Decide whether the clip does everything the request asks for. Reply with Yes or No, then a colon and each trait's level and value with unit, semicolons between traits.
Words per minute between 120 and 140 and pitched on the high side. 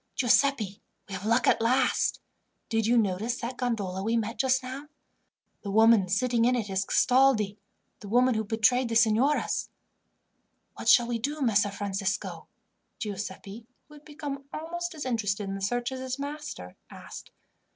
No: average, 160 wpm; high, 230 Hz